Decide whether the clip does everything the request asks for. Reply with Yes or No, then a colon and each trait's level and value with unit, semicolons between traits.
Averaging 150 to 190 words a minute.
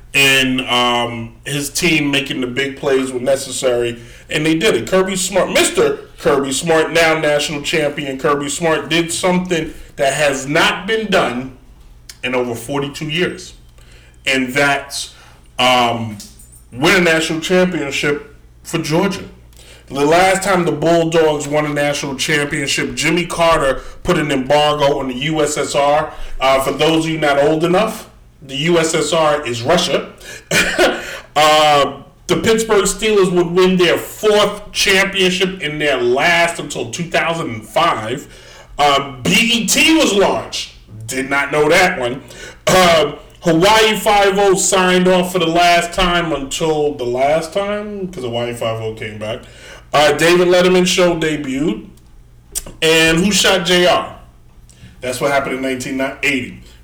No: slow, 135 wpm